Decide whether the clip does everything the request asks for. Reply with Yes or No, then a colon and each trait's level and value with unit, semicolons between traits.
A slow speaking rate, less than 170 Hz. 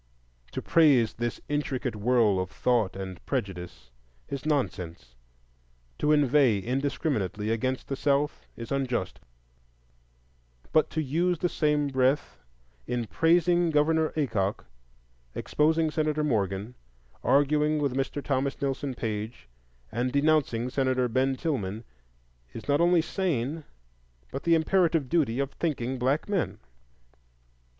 Yes: slow, 120 wpm; low, 135 Hz